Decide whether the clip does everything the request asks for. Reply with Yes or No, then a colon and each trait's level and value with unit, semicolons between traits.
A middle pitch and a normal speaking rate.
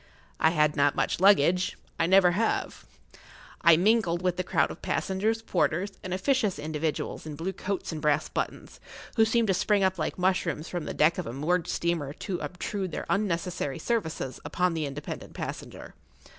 Yes: medium, 180 Hz; average, 170 wpm